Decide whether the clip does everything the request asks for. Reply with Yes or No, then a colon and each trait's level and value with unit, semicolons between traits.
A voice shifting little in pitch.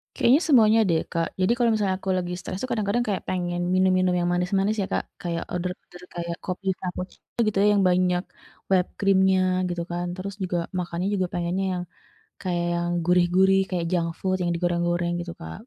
Yes: narrow, 1.7 semitones